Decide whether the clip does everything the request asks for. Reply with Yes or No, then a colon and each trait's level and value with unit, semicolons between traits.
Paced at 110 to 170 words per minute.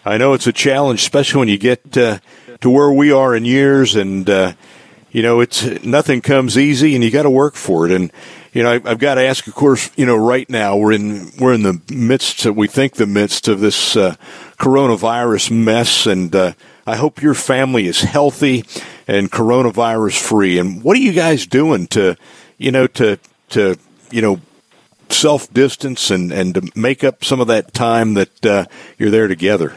No: fast, 205 wpm